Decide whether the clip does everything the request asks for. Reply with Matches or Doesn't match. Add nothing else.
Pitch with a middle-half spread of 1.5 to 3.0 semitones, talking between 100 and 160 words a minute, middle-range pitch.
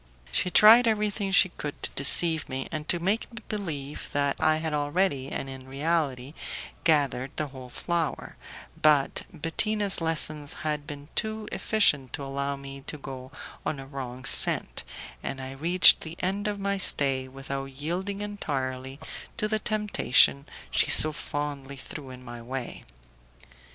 Doesn't match